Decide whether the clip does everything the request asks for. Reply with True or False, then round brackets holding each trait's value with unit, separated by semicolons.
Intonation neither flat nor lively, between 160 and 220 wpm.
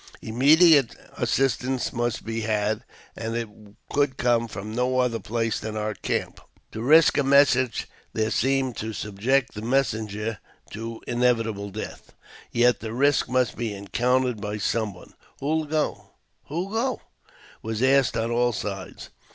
False (3.3 semitones; 150 wpm)